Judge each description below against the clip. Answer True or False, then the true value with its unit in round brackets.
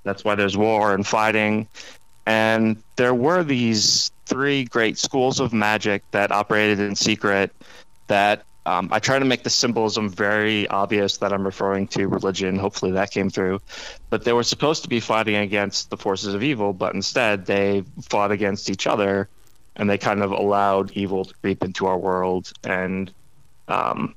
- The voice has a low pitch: True (105 Hz)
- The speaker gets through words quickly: False (175 wpm)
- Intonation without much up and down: True (2.1 semitones)